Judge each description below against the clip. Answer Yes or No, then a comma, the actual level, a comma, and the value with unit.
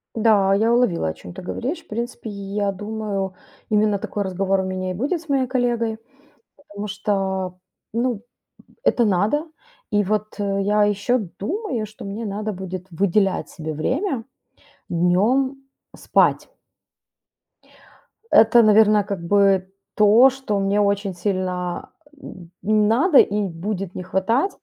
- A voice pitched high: Yes, high, 205 Hz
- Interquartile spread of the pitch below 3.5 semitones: Yes, average, 3.1 semitones